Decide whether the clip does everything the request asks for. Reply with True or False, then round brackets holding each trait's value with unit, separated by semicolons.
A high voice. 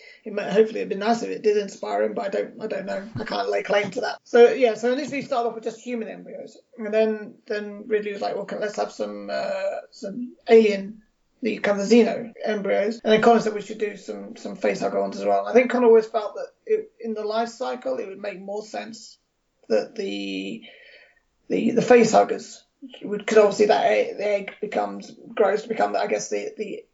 True (220 Hz)